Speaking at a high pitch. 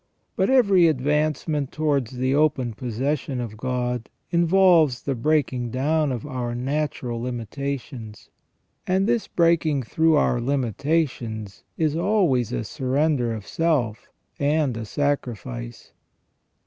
No: medium, 140 Hz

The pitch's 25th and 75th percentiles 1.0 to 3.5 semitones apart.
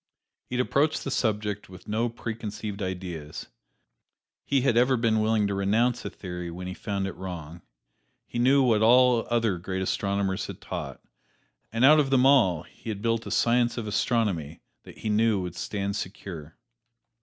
No: average, 4.0 semitones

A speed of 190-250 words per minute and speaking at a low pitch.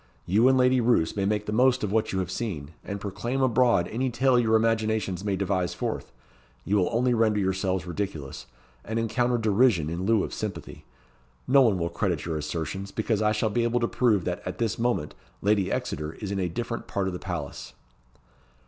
Yes: average, 200 wpm; low, 105 Hz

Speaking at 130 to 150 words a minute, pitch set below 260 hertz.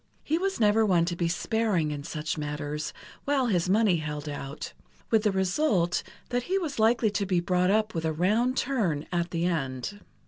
No: average, 195 wpm; medium, 185 Hz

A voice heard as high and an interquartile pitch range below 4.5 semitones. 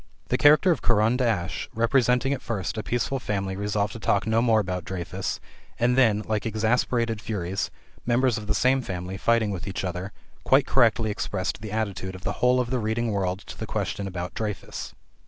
No: low, 110 Hz; average, 3.6 semitones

